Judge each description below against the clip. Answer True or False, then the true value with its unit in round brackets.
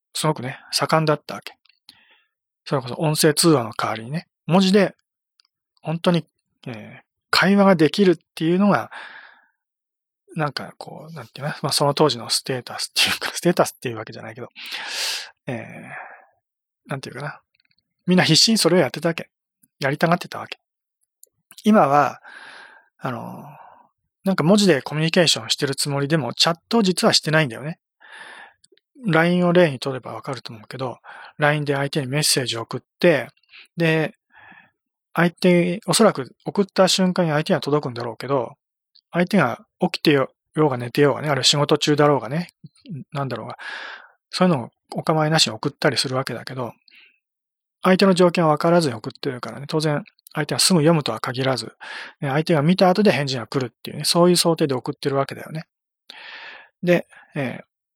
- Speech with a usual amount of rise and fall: True (4.6 semitones)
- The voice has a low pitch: False (160 Hz)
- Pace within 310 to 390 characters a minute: True (355 characters per minute)